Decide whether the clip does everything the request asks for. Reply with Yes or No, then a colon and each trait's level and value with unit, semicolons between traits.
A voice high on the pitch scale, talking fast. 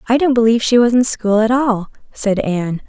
Yes: high, 225 Hz; fast, 230 wpm